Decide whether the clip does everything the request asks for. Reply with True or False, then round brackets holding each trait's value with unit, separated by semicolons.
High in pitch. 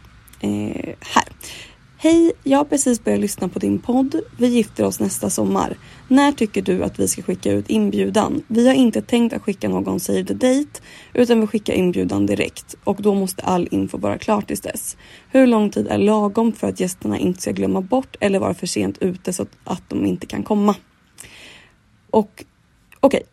True (205 Hz)